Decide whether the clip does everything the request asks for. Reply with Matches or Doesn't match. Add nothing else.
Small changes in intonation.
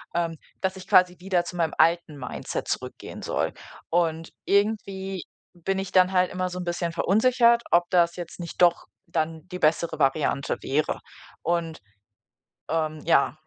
Matches